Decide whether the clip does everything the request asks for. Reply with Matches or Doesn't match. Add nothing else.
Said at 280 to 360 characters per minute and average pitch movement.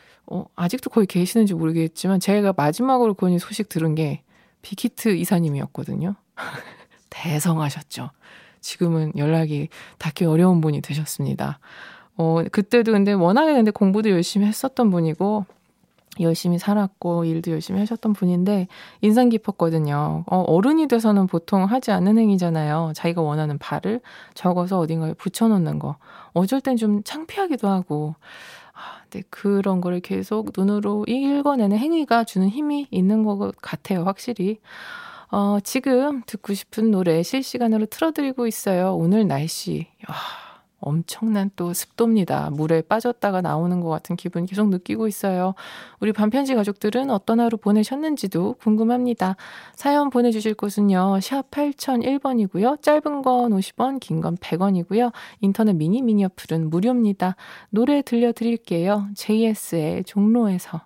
Matches